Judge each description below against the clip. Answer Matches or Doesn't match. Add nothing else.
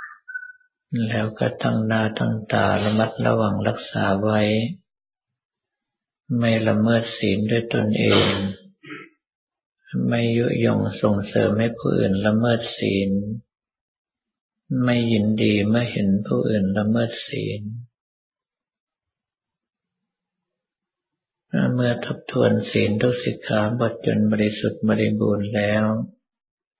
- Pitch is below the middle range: Matches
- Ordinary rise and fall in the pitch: Doesn't match